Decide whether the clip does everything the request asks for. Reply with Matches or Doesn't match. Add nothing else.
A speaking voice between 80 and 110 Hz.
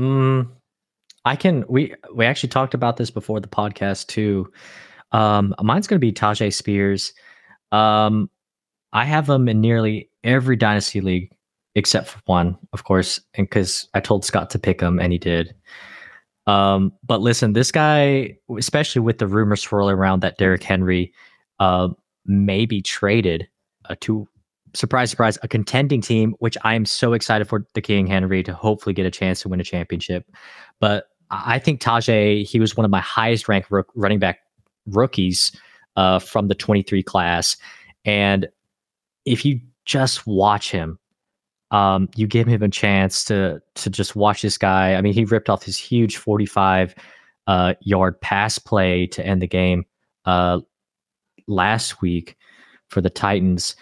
Matches